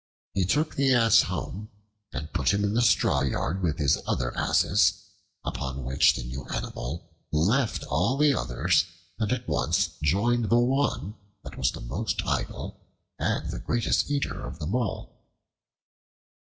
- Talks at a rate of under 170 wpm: Yes, average, 155 wpm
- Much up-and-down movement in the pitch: Yes, wide, 8.4 semitones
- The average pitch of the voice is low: Yes, low, 100 Hz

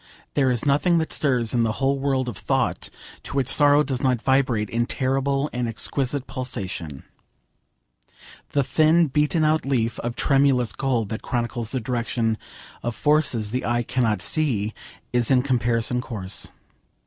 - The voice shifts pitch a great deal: No, average, 3.1 semitones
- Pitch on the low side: Yes, low, 125 Hz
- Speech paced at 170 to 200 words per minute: No, average, 155 wpm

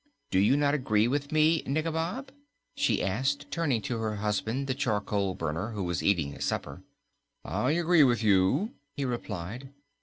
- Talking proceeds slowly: No, average, 160 wpm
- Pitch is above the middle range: No, low, 120 Hz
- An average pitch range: No, wide, 6.1 semitones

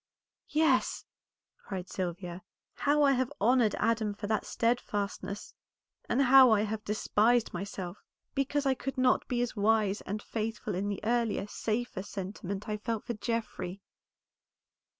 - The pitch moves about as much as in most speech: Yes, average, 3.3 semitones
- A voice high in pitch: Yes, high, 220 Hz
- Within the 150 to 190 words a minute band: No, average, 140 wpm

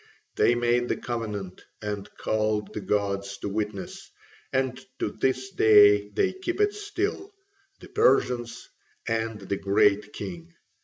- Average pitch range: Yes, average, 4.2 semitones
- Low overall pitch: Yes, low, 110 Hz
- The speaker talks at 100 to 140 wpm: Yes, slow, 135 wpm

